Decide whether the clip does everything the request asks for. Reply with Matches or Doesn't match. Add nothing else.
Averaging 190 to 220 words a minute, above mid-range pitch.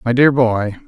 Doesn't match